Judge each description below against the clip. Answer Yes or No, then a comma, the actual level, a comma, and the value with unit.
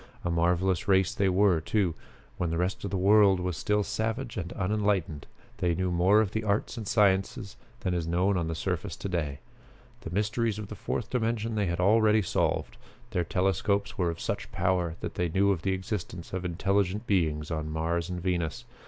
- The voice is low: Yes, very low, 95 Hz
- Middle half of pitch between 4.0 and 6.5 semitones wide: No, average, 3.1 semitones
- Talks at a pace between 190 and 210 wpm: Yes, average, 195 wpm